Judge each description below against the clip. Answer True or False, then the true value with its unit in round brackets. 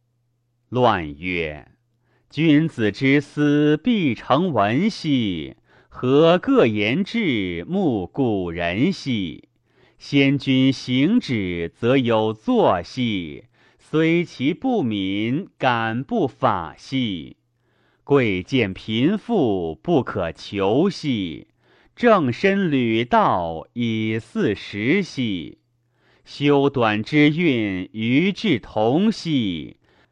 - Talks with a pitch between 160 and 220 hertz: False (125 Hz)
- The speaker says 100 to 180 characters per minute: True (115 characters per minute)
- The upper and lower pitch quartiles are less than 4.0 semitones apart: False (4.8 semitones)